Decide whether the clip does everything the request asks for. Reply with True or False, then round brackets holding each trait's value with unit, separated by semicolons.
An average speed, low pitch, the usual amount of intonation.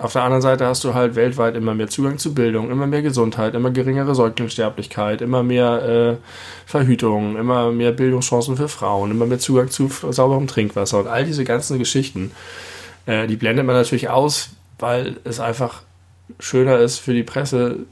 False (180 wpm; 120 Hz; 2.2 semitones)